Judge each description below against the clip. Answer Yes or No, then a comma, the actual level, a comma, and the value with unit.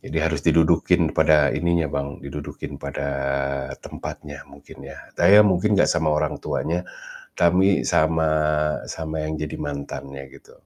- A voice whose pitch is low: Yes, very low, 80 Hz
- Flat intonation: No, average, 3.2 semitones